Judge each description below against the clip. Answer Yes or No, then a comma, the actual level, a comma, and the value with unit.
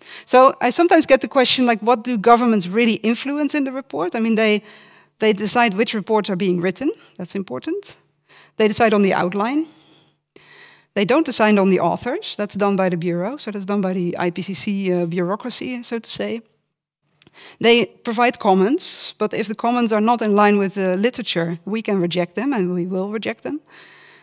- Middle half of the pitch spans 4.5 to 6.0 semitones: No, average, 4.0 semitones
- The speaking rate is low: No, average, 190 wpm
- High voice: Yes, high, 215 Hz